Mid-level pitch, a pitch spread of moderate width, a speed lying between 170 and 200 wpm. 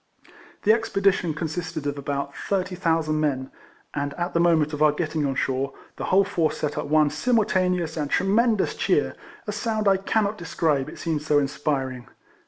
Yes: medium, 160 Hz; average, 4.7 semitones; average, 175 wpm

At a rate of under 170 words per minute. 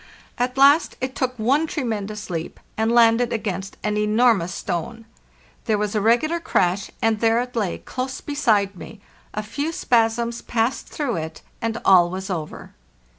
Yes: average, 160 wpm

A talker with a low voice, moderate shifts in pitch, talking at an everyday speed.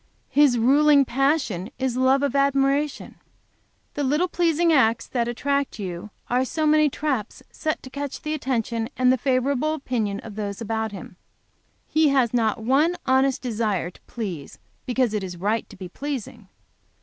No: very high, 260 Hz; average, 4.3 semitones; average, 160 wpm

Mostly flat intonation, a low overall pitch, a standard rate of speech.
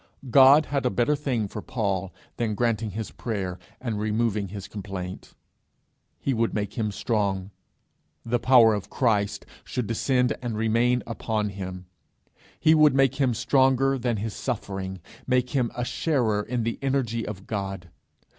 No: average, 3.7 semitones; low, 115 Hz; average, 155 wpm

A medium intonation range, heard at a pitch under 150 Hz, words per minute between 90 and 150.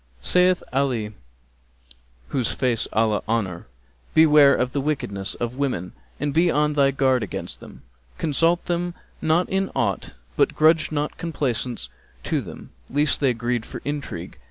Yes: average, 5.0 semitones; medium, 140 Hz; average, 145 wpm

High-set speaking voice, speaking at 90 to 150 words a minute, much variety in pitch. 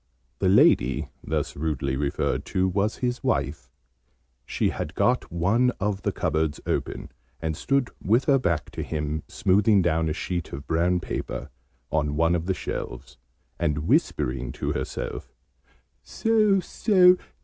No: very low, 85 Hz; average, 145 wpm; wide, 6.4 semitones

